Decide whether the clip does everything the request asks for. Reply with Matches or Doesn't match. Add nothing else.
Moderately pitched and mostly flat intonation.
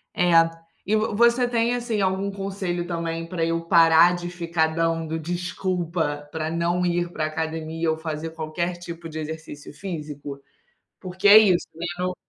Matches